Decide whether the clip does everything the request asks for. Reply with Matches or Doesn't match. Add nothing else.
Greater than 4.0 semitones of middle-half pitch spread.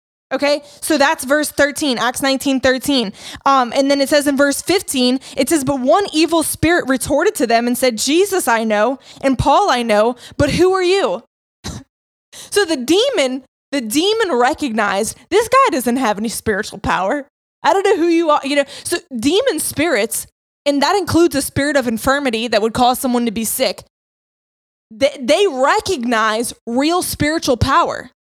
Matches